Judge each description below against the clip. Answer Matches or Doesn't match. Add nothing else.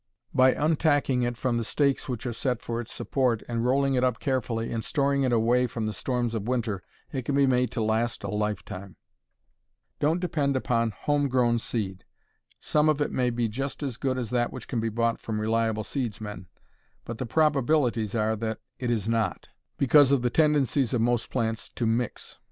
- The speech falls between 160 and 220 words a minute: Matches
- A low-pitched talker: Matches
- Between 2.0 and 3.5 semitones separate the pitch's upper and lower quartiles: Matches